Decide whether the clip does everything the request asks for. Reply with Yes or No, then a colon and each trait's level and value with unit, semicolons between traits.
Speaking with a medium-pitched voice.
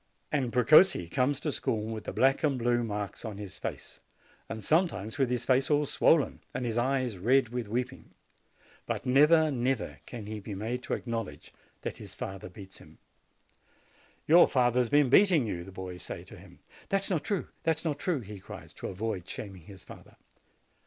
No: low, 120 Hz